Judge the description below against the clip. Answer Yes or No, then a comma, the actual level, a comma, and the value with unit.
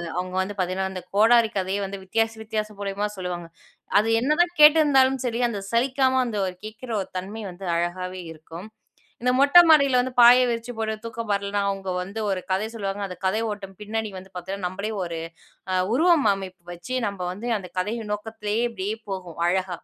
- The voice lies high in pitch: Yes, high, 210 Hz